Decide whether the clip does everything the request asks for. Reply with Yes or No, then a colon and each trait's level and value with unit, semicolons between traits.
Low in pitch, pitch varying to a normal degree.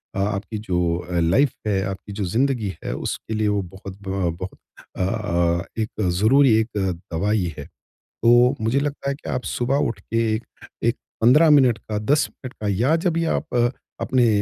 Yes: low, 110 Hz; average, 4.9 semitones